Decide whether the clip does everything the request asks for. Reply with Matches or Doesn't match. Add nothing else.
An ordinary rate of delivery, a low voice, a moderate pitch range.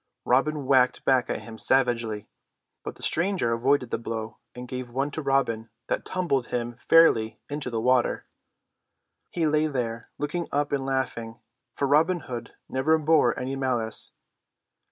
Matches